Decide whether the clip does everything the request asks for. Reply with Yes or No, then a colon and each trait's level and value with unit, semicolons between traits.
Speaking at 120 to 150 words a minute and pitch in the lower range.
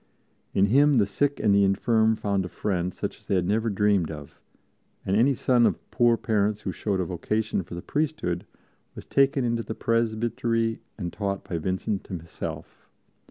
No: average, 180 wpm; low, 105 Hz